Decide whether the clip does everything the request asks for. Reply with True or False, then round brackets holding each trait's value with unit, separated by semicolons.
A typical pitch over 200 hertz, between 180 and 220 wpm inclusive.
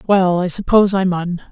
False (185 Hz; 200 wpm)